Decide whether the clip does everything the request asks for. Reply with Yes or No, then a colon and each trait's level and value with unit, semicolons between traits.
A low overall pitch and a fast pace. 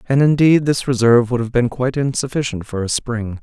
Yes: low, 125 Hz; fast, 210 wpm